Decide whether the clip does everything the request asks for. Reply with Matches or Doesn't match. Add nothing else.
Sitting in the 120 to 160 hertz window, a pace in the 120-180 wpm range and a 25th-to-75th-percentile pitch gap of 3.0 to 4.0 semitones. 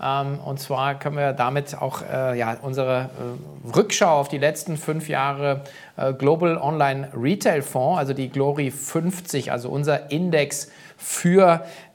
Doesn't match